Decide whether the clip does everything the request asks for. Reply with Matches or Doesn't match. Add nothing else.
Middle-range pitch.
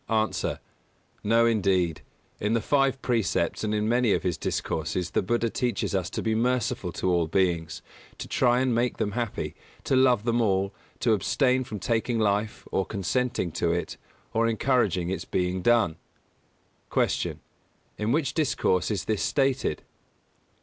Doesn't match